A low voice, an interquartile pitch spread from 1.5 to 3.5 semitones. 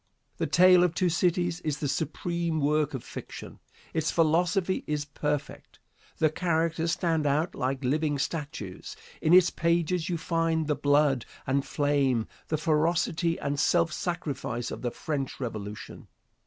No: medium, 155 Hz; average, 2.9 semitones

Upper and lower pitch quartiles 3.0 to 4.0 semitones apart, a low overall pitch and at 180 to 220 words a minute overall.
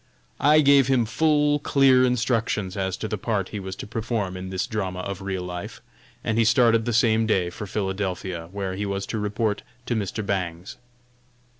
Yes: average, 3.6 semitones; low, 105 Hz; average, 185 wpm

